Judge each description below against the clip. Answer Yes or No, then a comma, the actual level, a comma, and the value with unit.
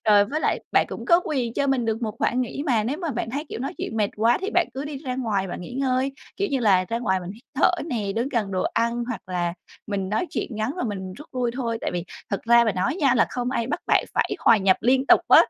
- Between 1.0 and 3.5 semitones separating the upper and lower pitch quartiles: No, average, 4.4 semitones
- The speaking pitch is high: Yes, high, 235 Hz